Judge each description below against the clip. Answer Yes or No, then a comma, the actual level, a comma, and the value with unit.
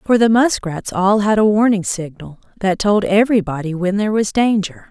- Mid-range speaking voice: No, high, 200 Hz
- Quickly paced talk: No, average, 185 wpm